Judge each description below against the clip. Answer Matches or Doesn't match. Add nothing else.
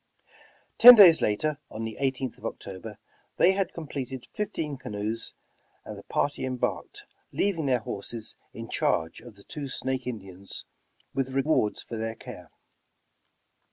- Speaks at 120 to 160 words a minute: Matches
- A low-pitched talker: Matches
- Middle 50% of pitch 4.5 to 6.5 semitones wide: Matches